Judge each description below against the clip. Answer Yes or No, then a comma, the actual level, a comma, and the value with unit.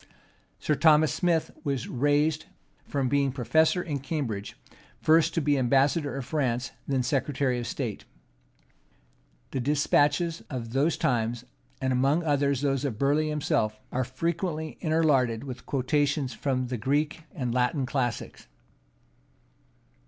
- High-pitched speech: No, medium, 140 Hz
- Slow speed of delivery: Yes, slow, 130 wpm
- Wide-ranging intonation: No, average, 3.1 semitones